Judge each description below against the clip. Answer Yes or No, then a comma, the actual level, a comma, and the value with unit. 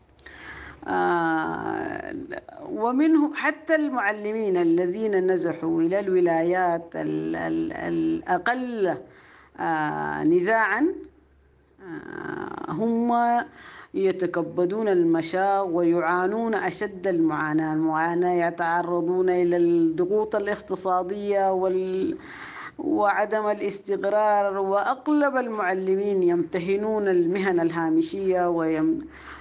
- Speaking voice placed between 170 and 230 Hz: Yes, high, 190 Hz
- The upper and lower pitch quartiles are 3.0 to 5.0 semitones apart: No, wide, 5.5 semitones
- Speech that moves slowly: Yes, slow, 65 wpm